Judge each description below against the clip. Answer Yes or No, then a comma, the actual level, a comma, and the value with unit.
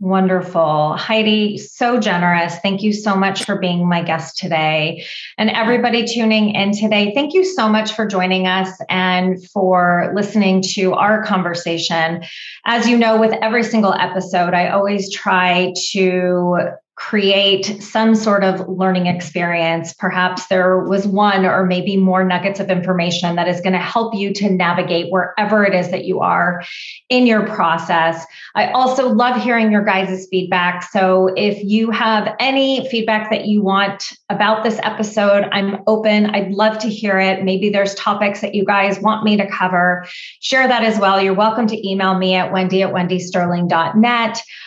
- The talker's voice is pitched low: No, high, 195 Hz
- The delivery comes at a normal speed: Yes, average, 165 wpm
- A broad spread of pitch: No, average, 2.9 semitones